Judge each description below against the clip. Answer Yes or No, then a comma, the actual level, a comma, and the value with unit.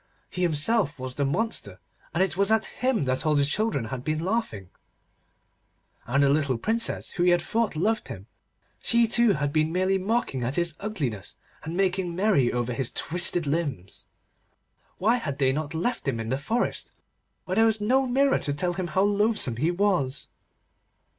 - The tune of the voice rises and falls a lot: Yes, wide, 7.2 semitones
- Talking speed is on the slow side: No, average, 180 wpm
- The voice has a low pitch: No, medium, 170 Hz